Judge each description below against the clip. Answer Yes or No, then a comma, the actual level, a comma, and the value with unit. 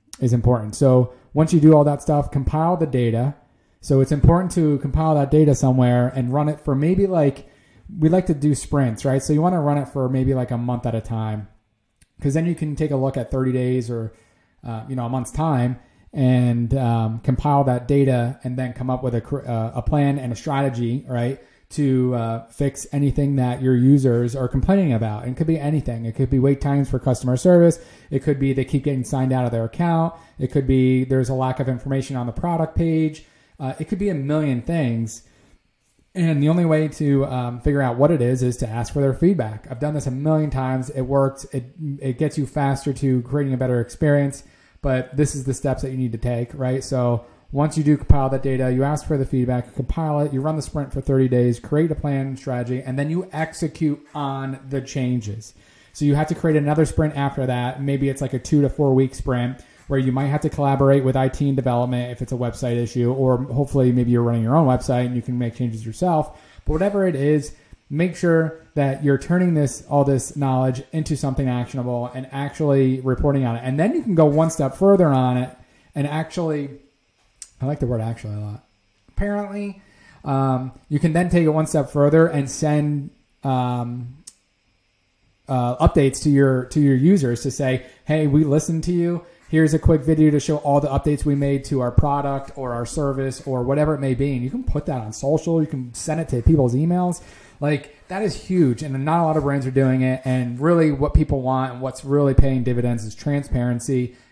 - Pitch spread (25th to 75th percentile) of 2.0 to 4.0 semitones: Yes, average, 3.0 semitones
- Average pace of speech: No, fast, 225 wpm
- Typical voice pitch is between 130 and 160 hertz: Yes, low, 135 Hz